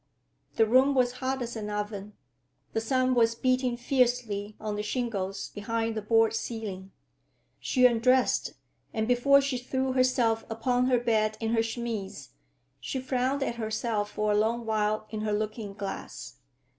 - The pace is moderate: Yes, average, 155 wpm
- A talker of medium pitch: No, high, 230 Hz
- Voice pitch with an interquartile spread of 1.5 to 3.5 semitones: Yes, average, 2.8 semitones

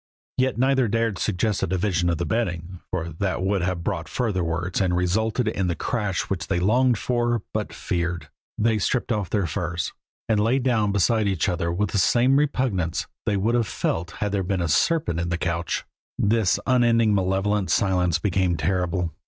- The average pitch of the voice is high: No, very low, 95 Hz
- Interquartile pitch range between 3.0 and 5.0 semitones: Yes, average, 4.4 semitones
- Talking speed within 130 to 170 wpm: No, average, 185 wpm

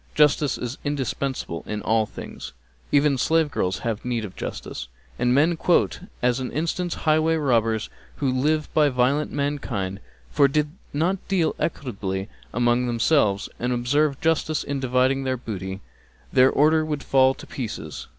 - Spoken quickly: No, average, 155 wpm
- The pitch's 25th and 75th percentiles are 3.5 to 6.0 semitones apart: Yes, average, 4.0 semitones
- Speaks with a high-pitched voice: No, low, 135 Hz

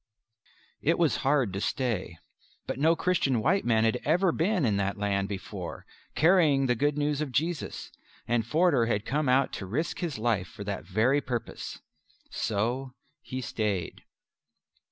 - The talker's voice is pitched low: Yes, low, 130 Hz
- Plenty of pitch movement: Yes, wide, 5.9 semitones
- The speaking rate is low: No, average, 155 wpm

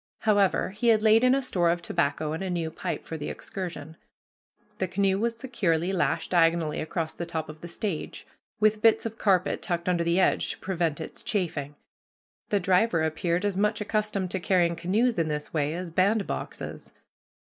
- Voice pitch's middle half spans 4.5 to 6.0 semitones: No, average, 3.9 semitones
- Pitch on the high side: No, medium, 180 Hz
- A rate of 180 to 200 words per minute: Yes, average, 185 wpm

